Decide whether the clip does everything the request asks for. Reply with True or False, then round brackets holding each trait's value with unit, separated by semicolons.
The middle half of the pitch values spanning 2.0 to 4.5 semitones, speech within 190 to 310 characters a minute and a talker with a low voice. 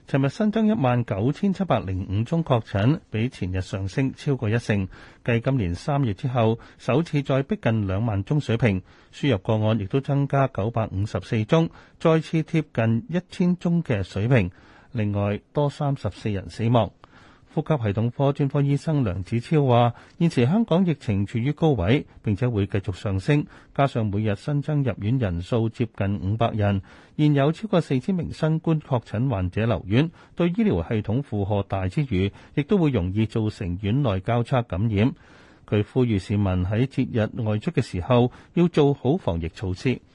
False (5.6 semitones; 265 characters per minute; 120 Hz)